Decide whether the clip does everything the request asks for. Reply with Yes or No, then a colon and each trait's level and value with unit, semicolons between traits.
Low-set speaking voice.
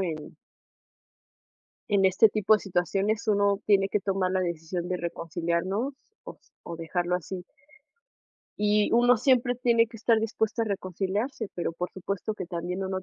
No: high, 195 Hz